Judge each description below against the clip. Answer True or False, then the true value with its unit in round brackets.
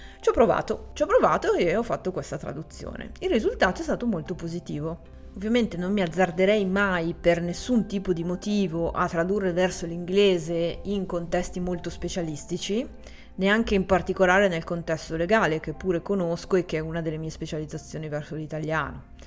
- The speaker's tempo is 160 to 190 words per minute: True (165 wpm)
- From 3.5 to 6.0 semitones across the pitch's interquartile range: False (3.0 semitones)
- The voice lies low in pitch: False (180 Hz)